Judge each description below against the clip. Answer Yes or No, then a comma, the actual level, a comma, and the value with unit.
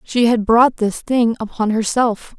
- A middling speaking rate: Yes, average, 175 wpm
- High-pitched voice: Yes, high, 230 Hz